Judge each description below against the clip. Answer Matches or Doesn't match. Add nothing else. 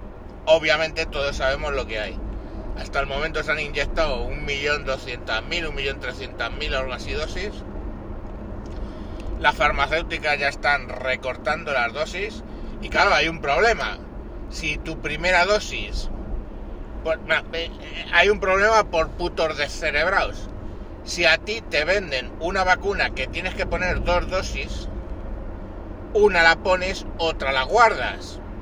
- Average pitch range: Doesn't match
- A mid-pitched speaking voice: Matches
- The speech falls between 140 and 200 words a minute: Doesn't match